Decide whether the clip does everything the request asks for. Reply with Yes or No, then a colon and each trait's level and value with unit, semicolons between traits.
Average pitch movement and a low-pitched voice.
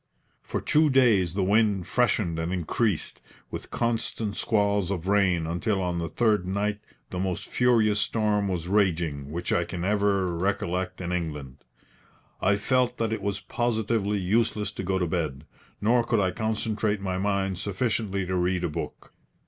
Yes: average, 3.2 semitones; low, 100 Hz